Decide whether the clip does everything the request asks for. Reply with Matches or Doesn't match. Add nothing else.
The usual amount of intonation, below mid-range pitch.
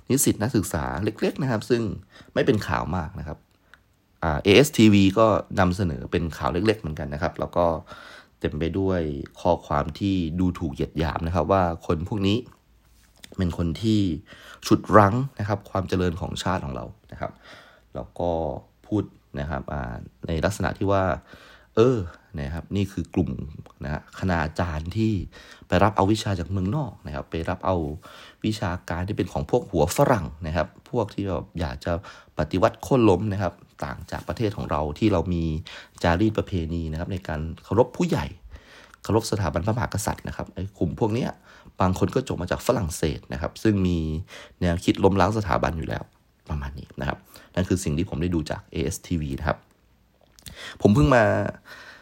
Matches